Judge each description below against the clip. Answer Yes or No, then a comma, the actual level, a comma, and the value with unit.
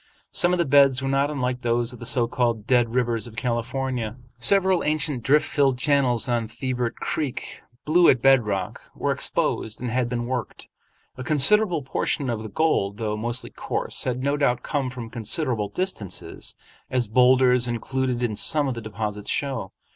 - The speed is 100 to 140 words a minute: No, average, 175 wpm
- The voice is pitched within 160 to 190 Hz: No, low, 125 Hz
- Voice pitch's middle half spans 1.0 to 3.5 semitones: Yes, average, 2.9 semitones